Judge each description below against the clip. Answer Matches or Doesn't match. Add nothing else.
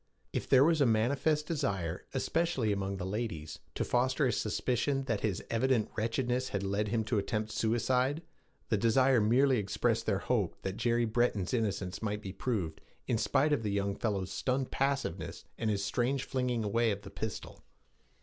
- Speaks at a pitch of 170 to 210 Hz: Doesn't match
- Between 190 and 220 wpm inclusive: Doesn't match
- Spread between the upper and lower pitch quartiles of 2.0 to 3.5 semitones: Doesn't match